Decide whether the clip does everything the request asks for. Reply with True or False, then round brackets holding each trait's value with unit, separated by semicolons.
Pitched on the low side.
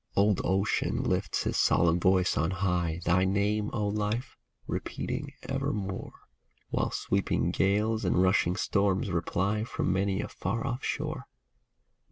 True (95 Hz)